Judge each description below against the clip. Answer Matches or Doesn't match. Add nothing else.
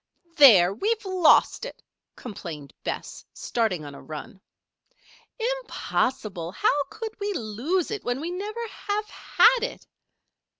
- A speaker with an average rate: Doesn't match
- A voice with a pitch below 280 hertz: Doesn't match